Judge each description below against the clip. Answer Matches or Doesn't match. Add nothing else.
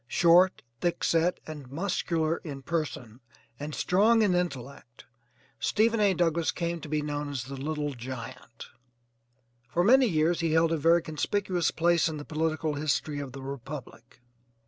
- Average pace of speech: Matches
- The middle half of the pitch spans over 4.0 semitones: Doesn't match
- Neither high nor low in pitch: Matches